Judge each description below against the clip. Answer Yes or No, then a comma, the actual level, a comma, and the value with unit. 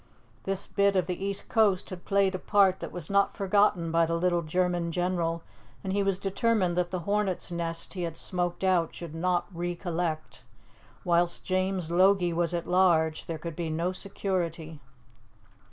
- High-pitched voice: No, medium, 180 Hz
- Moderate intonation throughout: No, narrow, 2.2 semitones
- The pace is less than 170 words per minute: No, average, 175 wpm